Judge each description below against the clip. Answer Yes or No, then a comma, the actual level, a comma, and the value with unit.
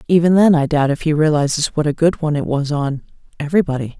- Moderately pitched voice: Yes, medium, 150 Hz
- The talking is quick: Yes, fast, 210 wpm